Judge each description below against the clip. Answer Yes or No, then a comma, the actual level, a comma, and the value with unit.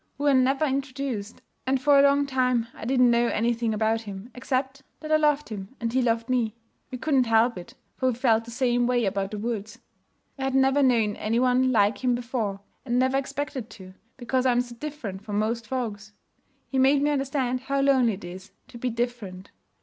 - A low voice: No, high, 245 Hz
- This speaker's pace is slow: No, fast, 205 wpm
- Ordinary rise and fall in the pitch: Yes, average, 3.1 semitones